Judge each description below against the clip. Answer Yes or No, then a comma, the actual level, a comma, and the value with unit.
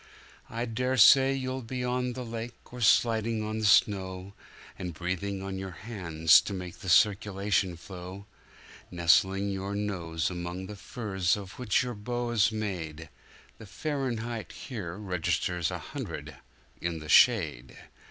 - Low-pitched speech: Yes, low, 100 Hz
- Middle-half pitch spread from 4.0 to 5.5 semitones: Yes, average, 4.3 semitones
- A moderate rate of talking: No, slow, 130 wpm